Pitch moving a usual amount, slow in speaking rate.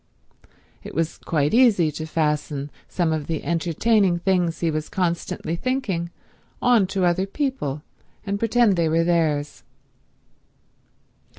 Yes: average, 3.9 semitones; slow, 125 wpm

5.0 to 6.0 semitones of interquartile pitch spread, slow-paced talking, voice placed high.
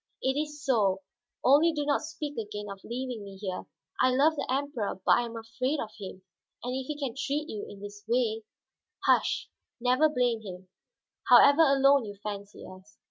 No: wide, 5.5 semitones; average, 190 wpm; high, 245 Hz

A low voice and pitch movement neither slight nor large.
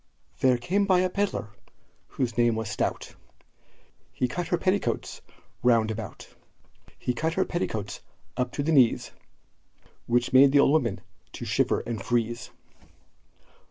No: low, 125 Hz; wide, 5.7 semitones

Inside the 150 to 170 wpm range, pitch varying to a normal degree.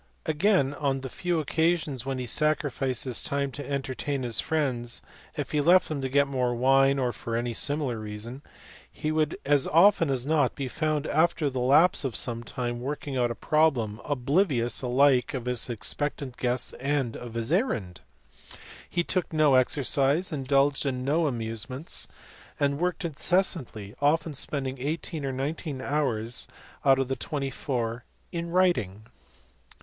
Yes: average, 160 wpm; average, 3.6 semitones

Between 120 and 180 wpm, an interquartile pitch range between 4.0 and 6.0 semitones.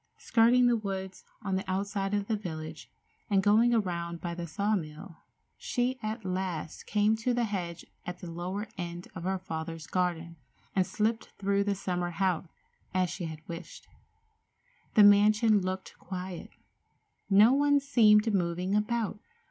No: average, 155 wpm; average, 3.4 semitones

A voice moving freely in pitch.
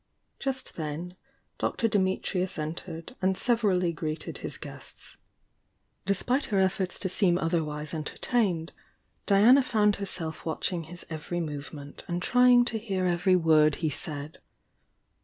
No: average, 4.1 semitones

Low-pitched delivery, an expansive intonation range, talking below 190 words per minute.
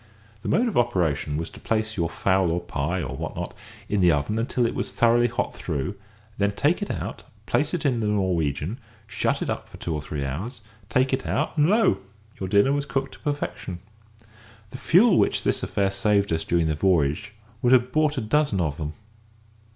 No: low, 100 Hz; wide, 7.5 semitones; fast, 205 wpm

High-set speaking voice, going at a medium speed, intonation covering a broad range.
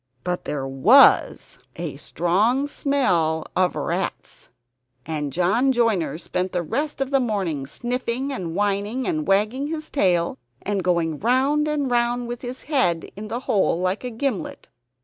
Yes: high, 215 Hz; average, 150 wpm; wide, 7.0 semitones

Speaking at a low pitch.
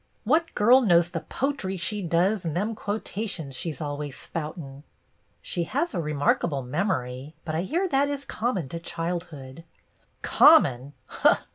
No: medium, 170 Hz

